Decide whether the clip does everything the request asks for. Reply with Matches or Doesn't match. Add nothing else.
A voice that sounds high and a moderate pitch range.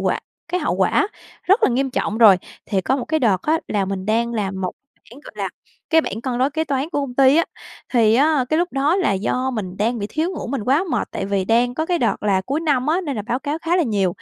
Doesn't match